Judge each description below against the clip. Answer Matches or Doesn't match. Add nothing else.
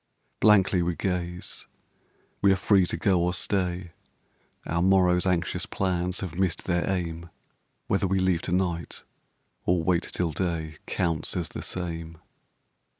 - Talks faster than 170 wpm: Doesn't match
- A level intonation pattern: Matches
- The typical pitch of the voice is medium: Doesn't match